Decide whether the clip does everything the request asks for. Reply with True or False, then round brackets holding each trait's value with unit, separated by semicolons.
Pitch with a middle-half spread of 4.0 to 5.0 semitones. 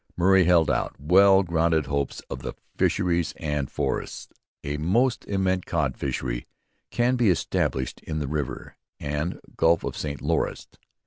True (4.3 semitones)